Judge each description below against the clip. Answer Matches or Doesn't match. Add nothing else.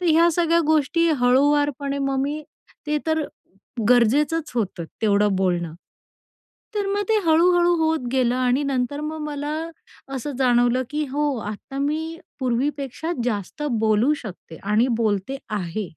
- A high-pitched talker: Matches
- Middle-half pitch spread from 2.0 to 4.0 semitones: Doesn't match